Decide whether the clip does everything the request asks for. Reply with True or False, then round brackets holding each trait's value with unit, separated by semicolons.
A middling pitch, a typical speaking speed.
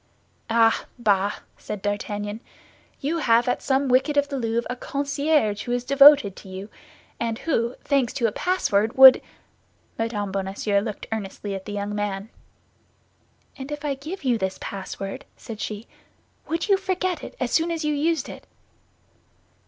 False (235 Hz; 160 wpm)